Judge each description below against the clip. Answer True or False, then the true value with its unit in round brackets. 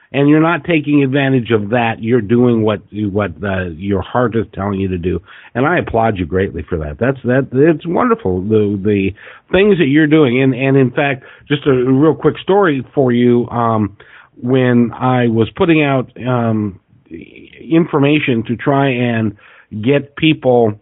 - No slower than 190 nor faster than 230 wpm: False (175 wpm)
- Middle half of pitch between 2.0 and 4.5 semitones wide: False (4.9 semitones)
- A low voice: True (125 Hz)